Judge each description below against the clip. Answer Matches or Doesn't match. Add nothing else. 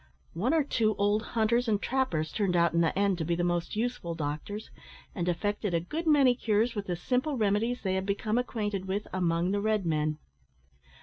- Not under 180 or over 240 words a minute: Matches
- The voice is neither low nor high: Doesn't match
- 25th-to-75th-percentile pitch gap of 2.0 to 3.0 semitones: Doesn't match